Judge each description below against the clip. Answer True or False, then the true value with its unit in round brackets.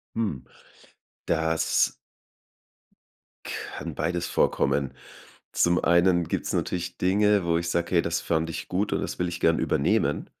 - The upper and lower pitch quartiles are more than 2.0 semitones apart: False (1.6 semitones)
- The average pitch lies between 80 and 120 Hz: True (85 Hz)